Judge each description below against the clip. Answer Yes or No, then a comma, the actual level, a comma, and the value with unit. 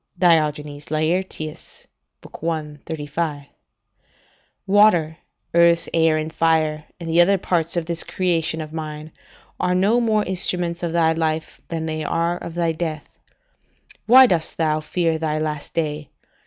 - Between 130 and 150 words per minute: Yes, average, 140 wpm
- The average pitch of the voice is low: No, medium, 165 Hz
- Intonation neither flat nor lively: No, narrow, 1.8 semitones